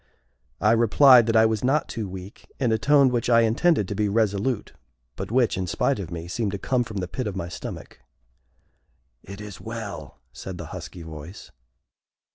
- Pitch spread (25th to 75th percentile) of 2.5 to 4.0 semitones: Yes, average, 3.6 semitones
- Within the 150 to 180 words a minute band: No, average, 190 wpm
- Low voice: Yes, low, 110 Hz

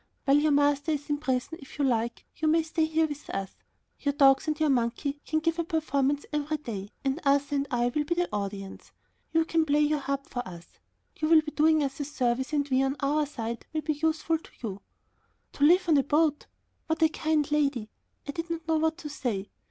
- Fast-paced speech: Yes, fast, 225 wpm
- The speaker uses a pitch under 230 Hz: No, very high, 290 Hz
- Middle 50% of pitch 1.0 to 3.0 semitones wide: Yes, average, 2.7 semitones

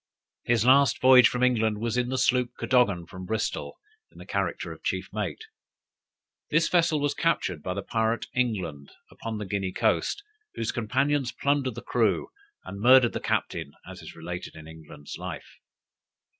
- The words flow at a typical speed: Yes, average, 165 wpm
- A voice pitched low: Yes, low, 115 Hz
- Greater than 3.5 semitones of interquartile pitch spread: Yes, average, 5.3 semitones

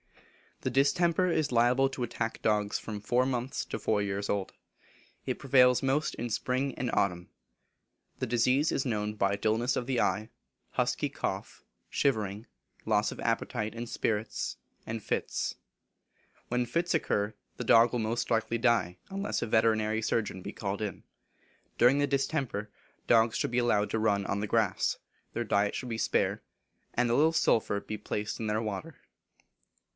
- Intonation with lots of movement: No, average, 3.1 semitones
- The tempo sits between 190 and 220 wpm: No, average, 165 wpm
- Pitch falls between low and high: No, low, 115 Hz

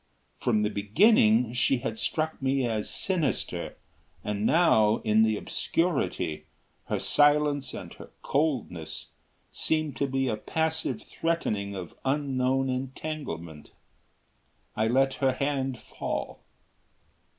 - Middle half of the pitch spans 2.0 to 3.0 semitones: No, average, 5.2 semitones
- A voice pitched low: Yes, low, 130 Hz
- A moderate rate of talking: No, slow, 115 wpm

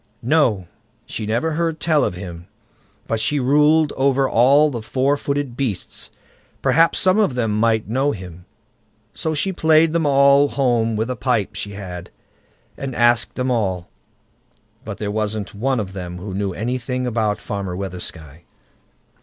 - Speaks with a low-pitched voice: Yes, low, 120 Hz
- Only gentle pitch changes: No, wide, 5.6 semitones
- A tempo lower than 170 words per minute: Yes, average, 155 wpm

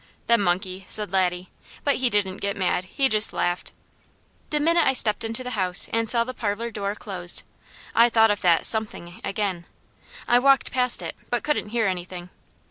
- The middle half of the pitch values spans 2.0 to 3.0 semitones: No, average, 4.3 semitones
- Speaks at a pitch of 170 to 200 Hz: No, high, 210 Hz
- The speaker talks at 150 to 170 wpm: No, average, 185 wpm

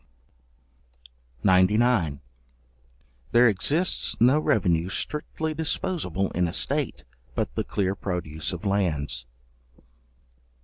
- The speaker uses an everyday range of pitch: No, wide, 6.6 semitones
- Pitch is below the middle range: Yes, very low, 95 Hz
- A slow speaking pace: Yes, slow, 90 wpm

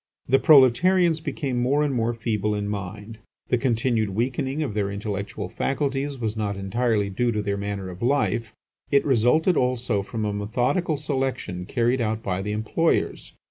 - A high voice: No, low, 115 Hz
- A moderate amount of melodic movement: Yes, average, 4.6 semitones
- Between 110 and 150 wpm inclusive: No, average, 165 wpm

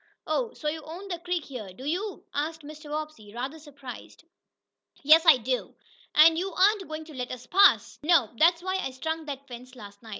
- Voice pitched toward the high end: Yes, very high, 305 Hz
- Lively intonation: No, average, 4.5 semitones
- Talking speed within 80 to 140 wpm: No, average, 200 wpm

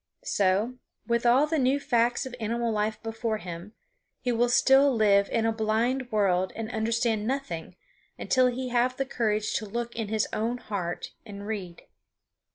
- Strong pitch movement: No, average, 2.7 semitones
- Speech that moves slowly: No, average, 165 wpm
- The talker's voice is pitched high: Yes, high, 225 Hz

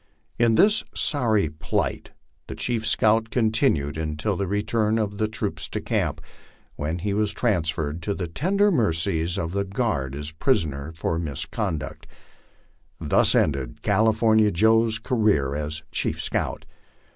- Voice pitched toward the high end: No, low, 100 Hz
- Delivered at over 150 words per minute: No, average, 145 wpm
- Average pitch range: No, wide, 5.8 semitones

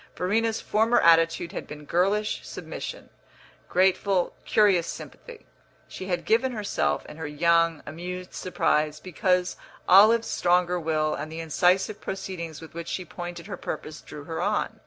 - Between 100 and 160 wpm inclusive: Yes, average, 145 wpm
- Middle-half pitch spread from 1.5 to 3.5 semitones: Yes, average, 3.2 semitones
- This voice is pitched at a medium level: Yes, medium, 180 Hz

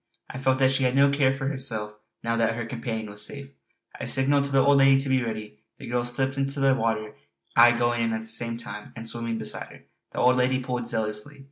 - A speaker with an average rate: No, fast, 240 wpm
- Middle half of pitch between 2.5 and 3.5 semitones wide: Yes, average, 2.9 semitones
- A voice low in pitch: Yes, low, 120 Hz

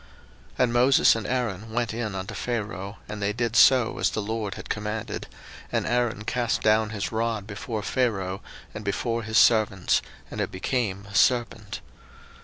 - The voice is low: Yes, low, 110 Hz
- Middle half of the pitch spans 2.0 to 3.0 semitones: Yes, narrow, 2.6 semitones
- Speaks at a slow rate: No, average, 170 wpm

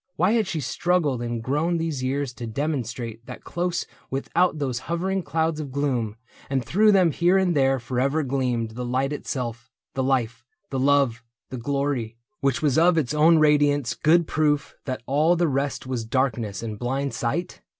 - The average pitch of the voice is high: No, medium, 140 Hz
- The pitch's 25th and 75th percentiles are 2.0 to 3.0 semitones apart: No, average, 4.3 semitones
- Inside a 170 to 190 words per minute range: Yes, average, 175 wpm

